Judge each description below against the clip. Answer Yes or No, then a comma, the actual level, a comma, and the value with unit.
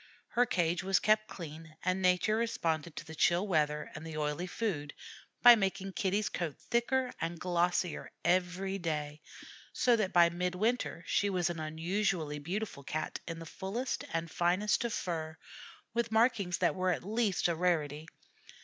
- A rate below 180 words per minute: Yes, average, 160 wpm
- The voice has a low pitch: No, medium, 180 Hz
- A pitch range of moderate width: Yes, average, 4.0 semitones